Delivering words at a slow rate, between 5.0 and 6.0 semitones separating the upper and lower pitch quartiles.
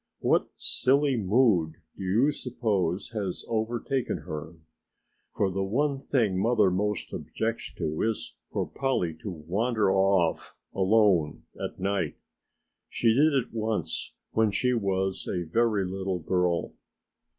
No: slow, 130 wpm; average, 4.0 semitones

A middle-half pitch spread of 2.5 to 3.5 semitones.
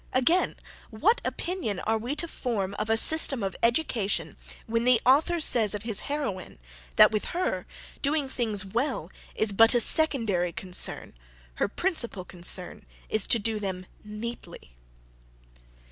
No: wide, 5.5 semitones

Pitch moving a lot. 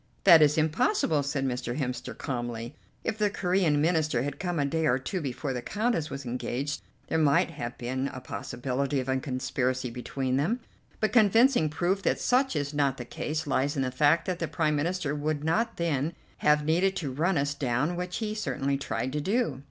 No: average, 4.7 semitones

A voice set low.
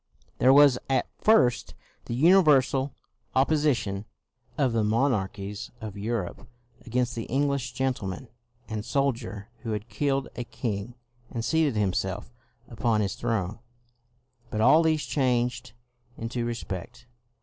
Yes: low, 120 Hz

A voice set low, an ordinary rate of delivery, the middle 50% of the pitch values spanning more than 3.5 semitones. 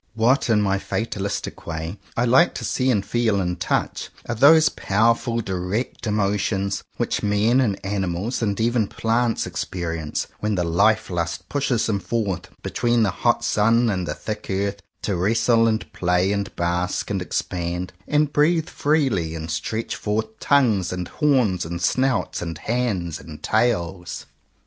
Yes: low, 105 Hz; average, 160 wpm; average, 4.6 semitones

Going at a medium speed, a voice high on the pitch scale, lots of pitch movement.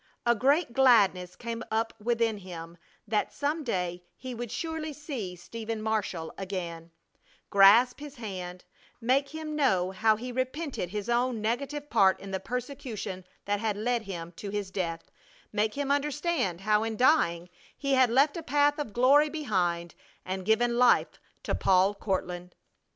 Yes: average, 155 wpm; high, 225 Hz; wide, 5.8 semitones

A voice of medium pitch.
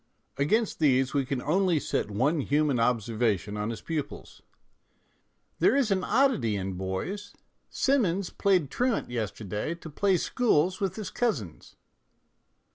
Yes: medium, 150 Hz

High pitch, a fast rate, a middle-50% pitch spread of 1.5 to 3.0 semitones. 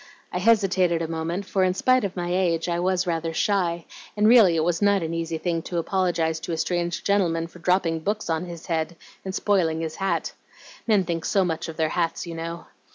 No: medium, 175 Hz; fast, 220 wpm; narrow, 2.4 semitones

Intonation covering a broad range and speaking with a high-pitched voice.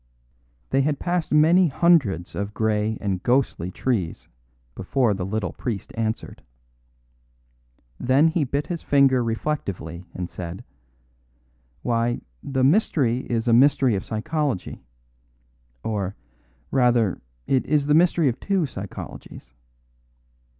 No: wide, 6.0 semitones; low, 120 Hz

